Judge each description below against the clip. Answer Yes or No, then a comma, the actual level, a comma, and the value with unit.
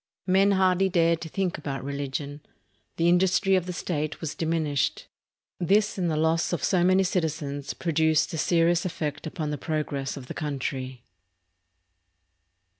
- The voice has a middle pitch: Yes, medium, 160 Hz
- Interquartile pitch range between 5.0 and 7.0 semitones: No, average, 3.6 semitones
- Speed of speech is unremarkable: Yes, average, 150 wpm